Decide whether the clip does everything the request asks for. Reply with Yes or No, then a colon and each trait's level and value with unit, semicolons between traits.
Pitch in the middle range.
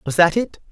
Yes: medium, 175 Hz